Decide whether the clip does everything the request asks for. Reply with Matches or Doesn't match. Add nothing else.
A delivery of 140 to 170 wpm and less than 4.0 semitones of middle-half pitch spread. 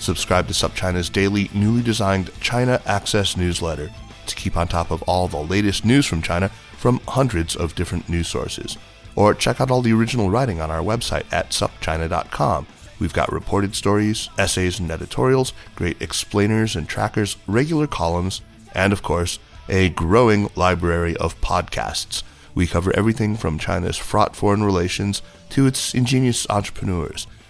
Doesn't match